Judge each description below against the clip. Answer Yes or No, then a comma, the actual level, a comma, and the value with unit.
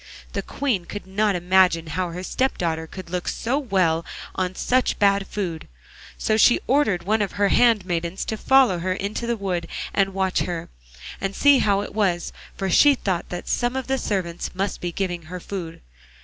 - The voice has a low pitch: No, high, 190 Hz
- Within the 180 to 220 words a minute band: Yes, average, 190 wpm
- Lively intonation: No, average, 3.4 semitones